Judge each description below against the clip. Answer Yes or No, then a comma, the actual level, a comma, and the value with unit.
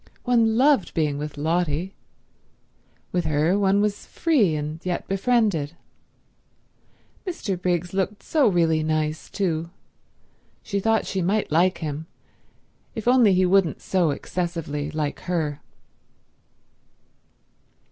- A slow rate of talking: Yes, slow, 115 wpm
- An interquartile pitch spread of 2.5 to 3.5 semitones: No, average, 4.4 semitones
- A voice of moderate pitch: Yes, medium, 180 Hz